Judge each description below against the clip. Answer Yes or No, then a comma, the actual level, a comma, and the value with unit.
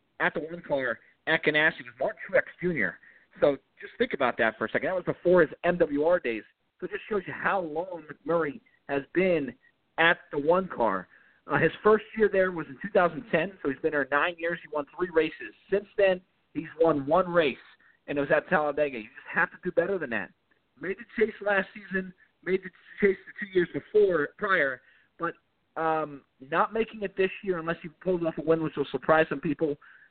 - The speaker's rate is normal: No, fast, 210 wpm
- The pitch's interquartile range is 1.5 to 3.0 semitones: No, average, 3.7 semitones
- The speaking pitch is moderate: Yes, medium, 170 Hz